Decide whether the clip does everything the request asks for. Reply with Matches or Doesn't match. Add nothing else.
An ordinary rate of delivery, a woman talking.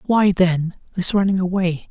Doesn't match